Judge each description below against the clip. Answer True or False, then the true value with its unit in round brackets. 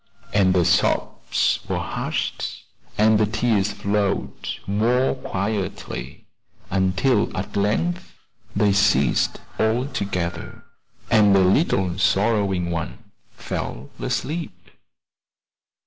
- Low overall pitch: True (100 Hz)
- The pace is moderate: False (85 wpm)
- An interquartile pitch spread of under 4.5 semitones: True (2.9 semitones)